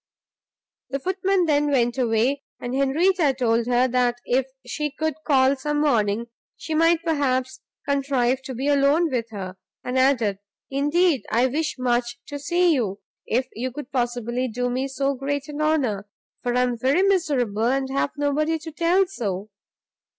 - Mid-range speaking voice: No, very high, 270 Hz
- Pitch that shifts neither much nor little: Yes, average, 3.5 semitones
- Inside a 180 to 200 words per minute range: No, average, 165 wpm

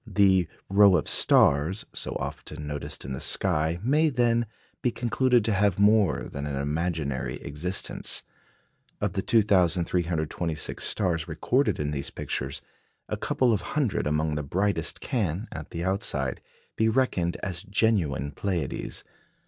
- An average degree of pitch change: No, wide, 5.9 semitones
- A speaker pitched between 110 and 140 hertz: No, very low, 90 Hz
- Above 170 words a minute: No, average, 140 wpm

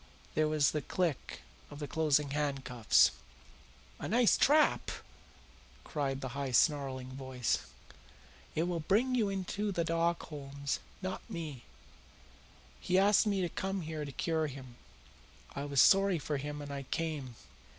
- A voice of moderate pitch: Yes, medium, 150 Hz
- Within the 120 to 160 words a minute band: Yes, average, 145 wpm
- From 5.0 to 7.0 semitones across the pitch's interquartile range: No, average, 4.6 semitones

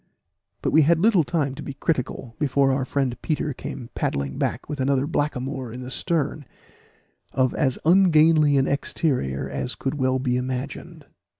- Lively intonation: No, average, 3.0 semitones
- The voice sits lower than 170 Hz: Yes, low, 135 Hz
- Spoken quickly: No, average, 165 wpm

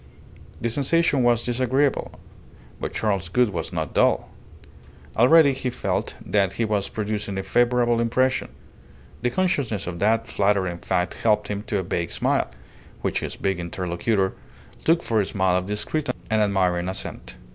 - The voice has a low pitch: Yes, low, 105 Hz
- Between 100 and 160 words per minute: Yes, average, 155 wpm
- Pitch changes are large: No, average, 4.4 semitones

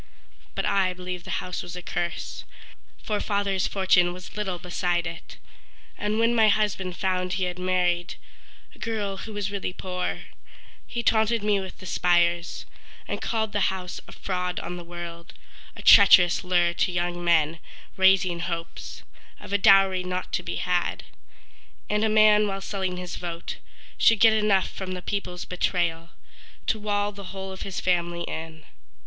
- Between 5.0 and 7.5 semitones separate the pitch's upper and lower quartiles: No, narrow, 2.4 semitones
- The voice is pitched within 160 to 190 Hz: Yes, medium, 185 Hz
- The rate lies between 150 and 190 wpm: Yes, average, 165 wpm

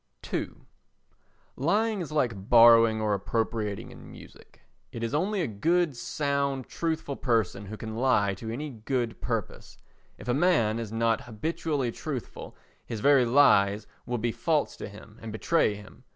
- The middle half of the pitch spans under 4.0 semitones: No, average, 4.8 semitones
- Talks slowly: No, average, 155 wpm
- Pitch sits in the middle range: No, low, 120 Hz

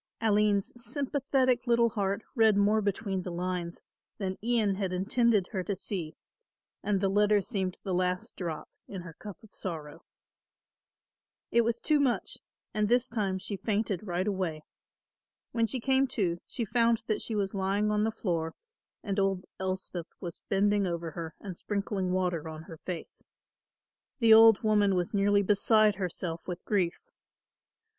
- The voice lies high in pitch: Yes, high, 200 Hz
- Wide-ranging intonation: No, average, 3.2 semitones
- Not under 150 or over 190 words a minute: Yes, average, 160 wpm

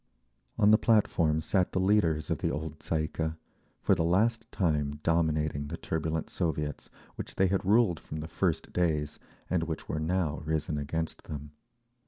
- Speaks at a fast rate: No, average, 170 wpm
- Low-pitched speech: Yes, very low, 80 Hz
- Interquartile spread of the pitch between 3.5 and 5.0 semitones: No, average, 3.0 semitones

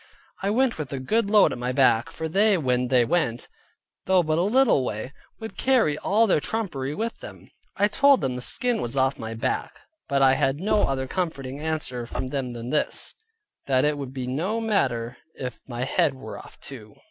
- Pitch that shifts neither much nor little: No, wide, 7.7 semitones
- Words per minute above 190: Yes, fast, 205 wpm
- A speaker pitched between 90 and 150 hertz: Yes, medium, 140 Hz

